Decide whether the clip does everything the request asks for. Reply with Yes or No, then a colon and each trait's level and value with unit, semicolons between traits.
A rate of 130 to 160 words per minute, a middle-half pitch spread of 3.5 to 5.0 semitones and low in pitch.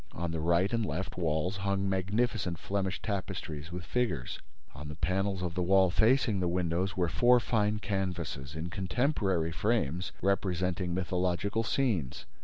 No: average, 150 wpm; average, 2.8 semitones; very low, 95 Hz